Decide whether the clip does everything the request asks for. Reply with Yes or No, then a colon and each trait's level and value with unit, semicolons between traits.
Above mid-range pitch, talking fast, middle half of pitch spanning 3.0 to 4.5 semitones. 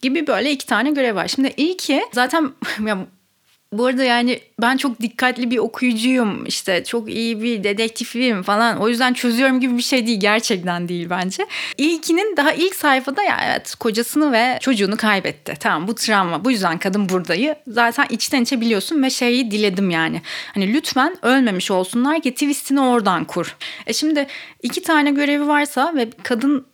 Yes: high, 245 Hz; fast, 170 wpm; average, 4.2 semitones